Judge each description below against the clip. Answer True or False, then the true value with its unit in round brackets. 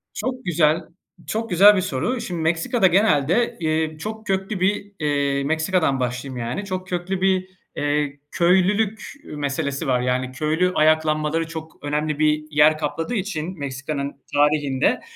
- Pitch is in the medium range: True (160 Hz)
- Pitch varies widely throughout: False (4.3 semitones)